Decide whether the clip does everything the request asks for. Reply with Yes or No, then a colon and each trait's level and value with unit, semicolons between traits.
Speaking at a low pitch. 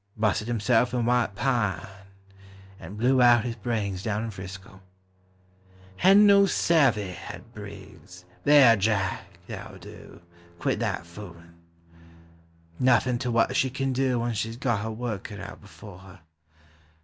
Yes: low, 110 Hz